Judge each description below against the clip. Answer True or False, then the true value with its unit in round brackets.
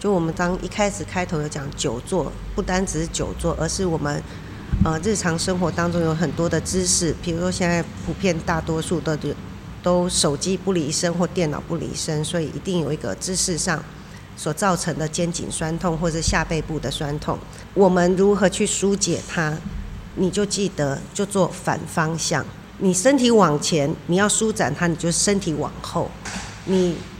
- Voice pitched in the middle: True (170 Hz)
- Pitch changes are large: False (2.7 semitones)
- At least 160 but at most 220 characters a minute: False (265 characters per minute)